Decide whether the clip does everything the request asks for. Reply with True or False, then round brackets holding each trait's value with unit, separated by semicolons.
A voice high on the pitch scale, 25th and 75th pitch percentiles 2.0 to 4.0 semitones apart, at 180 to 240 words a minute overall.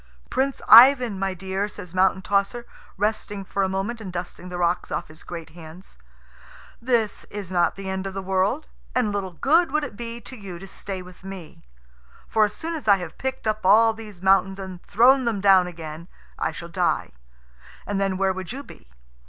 True (195 Hz; 3.3 semitones; 200 wpm)